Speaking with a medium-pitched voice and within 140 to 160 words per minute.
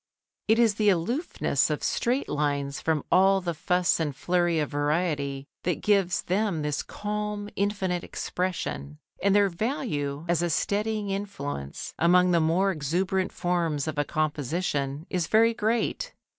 Yes: medium, 180 Hz; average, 145 wpm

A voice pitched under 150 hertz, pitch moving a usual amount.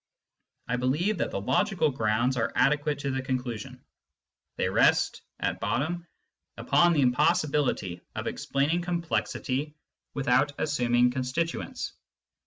Yes: medium, 140 Hz; average, 4.5 semitones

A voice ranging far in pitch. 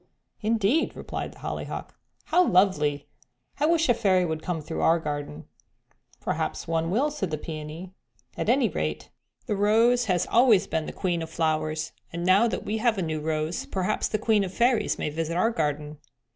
Yes: wide, 5.9 semitones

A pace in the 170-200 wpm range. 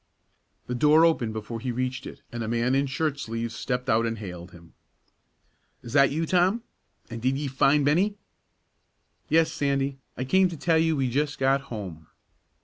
Yes: average, 180 wpm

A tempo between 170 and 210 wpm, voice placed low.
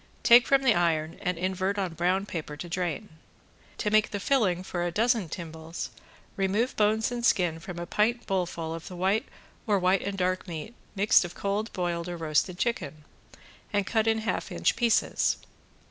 No: average, 180 wpm; medium, 185 Hz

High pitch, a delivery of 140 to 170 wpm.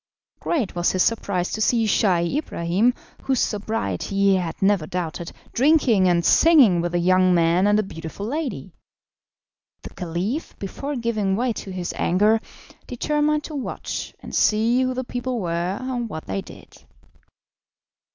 Yes: high, 205 Hz; average, 150 wpm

